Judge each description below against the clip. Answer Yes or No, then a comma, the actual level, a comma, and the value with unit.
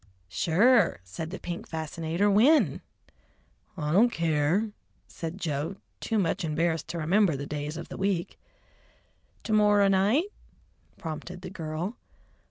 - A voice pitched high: No, medium, 175 Hz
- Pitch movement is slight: No, average, 4.2 semitones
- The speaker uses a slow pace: Yes, slow, 130 wpm